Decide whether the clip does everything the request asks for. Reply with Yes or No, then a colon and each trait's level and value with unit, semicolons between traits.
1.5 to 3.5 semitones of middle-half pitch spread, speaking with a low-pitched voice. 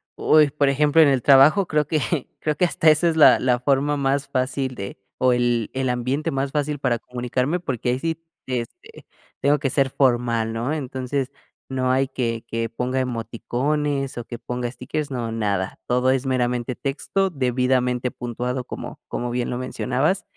Yes: average, 2.8 semitones; low, 130 Hz